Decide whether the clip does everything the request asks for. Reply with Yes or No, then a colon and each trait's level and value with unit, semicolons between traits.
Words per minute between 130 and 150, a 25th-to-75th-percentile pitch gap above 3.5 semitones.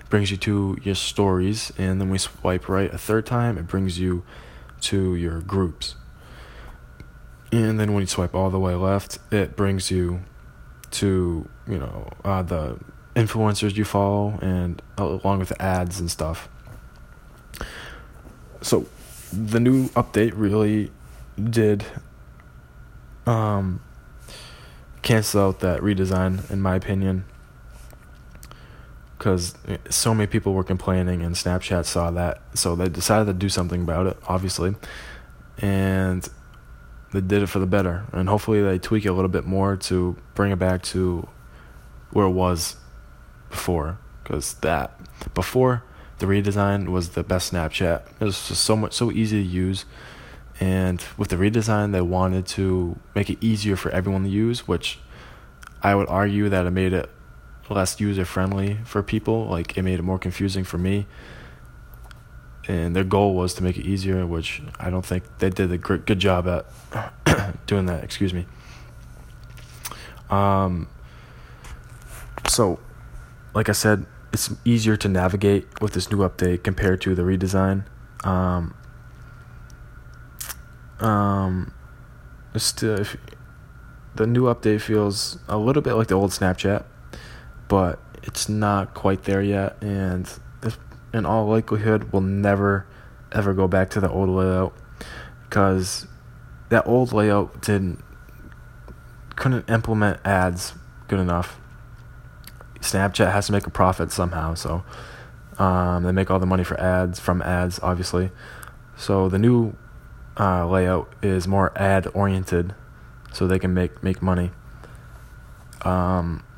No: average, 140 wpm; narrow, 2.5 semitones